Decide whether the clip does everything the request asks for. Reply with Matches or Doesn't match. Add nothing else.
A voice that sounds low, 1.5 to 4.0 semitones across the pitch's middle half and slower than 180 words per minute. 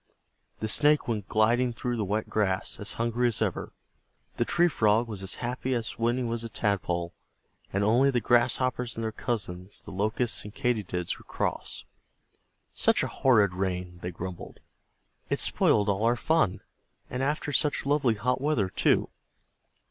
Matches